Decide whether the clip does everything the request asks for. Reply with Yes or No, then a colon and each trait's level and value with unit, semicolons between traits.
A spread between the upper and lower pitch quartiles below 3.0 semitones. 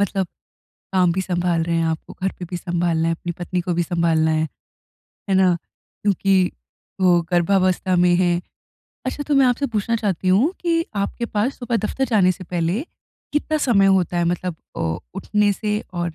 No: average, 3.3 semitones